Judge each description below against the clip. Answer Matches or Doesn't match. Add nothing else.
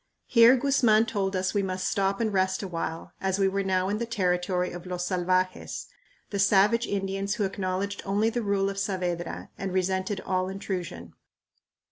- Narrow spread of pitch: Matches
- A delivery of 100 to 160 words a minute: Doesn't match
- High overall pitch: Matches